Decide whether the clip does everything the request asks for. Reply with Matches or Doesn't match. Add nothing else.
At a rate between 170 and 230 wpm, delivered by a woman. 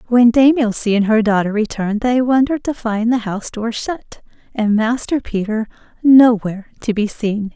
Matches